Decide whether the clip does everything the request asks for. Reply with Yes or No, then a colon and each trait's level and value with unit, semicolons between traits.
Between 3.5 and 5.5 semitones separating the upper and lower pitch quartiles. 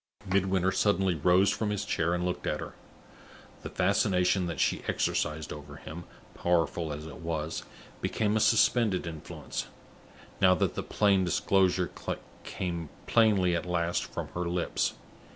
No: narrow, 2.4 semitones